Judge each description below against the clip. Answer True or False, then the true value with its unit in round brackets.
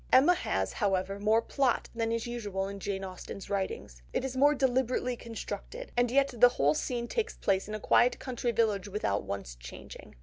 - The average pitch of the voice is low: False (225 Hz)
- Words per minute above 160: True (190 wpm)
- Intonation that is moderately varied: True (4.5 semitones)